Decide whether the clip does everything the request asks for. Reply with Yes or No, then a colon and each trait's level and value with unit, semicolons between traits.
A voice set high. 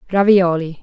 No: medium, 180 Hz